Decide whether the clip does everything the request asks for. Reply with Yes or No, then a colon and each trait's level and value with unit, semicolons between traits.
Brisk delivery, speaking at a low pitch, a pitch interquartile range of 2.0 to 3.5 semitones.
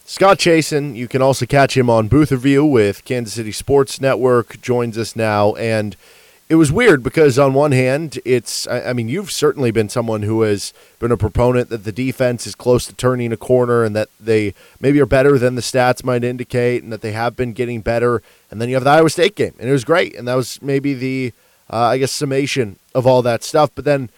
Yes: fast, 230 wpm; low, 125 Hz; average, 2.8 semitones